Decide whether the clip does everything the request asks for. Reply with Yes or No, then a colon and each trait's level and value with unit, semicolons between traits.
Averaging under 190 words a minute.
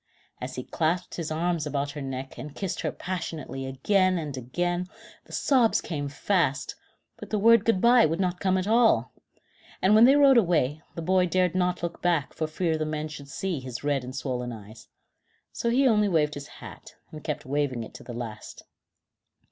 No: average, 195 wpm